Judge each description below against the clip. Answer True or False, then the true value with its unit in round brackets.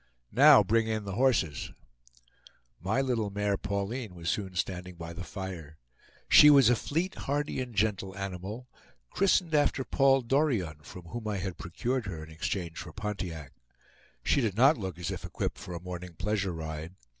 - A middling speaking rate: True (170 wpm)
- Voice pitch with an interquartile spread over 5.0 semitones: True (5.6 semitones)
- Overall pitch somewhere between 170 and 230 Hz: False (100 Hz)